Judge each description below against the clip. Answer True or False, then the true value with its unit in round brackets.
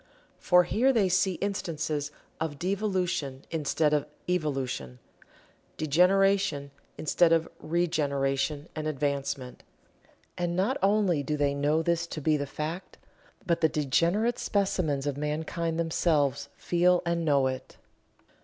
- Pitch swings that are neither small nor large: True (3.9 semitones)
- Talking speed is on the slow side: True (125 wpm)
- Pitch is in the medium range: True (160 Hz)